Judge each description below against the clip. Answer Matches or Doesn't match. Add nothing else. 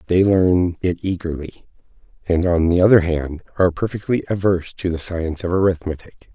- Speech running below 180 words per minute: Matches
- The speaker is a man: Matches